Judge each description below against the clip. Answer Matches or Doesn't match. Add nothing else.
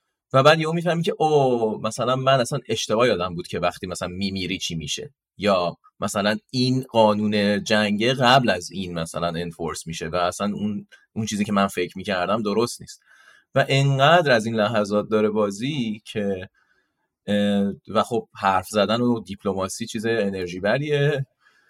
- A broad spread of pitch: Doesn't match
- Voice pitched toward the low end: Matches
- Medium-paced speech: Doesn't match